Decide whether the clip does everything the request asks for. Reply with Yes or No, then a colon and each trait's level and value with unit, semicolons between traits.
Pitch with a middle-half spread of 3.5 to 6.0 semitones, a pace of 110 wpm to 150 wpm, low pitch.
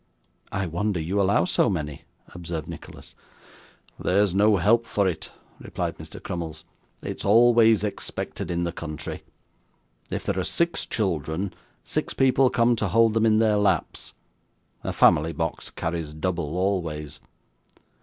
Yes: average, 4.5 semitones; average, 140 wpm; very low, 95 Hz